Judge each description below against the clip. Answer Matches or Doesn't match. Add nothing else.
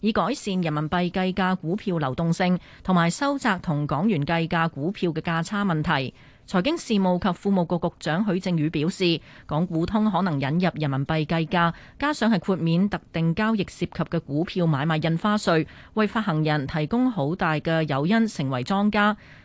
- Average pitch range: Matches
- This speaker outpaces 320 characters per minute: Doesn't match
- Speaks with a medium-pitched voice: Matches